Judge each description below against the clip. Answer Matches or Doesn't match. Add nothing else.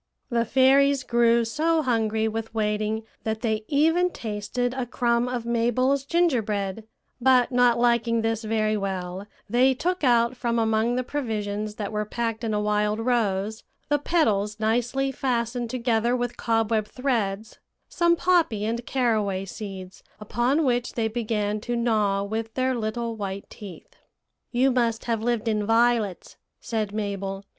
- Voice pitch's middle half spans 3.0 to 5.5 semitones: Doesn't match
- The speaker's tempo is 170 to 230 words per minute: Doesn't match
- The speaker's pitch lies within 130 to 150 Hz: Doesn't match